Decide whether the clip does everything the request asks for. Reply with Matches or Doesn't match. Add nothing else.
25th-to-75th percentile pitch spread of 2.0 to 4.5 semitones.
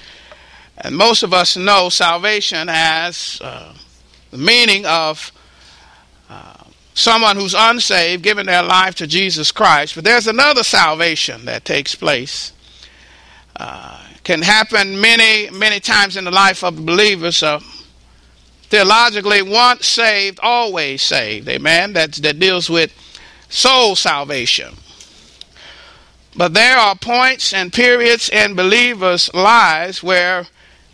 Doesn't match